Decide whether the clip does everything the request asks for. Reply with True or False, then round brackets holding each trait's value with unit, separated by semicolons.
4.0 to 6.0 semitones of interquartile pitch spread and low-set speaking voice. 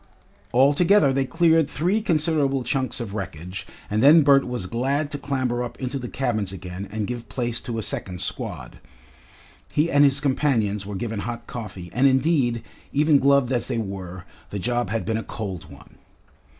True (4.7 semitones; 125 Hz)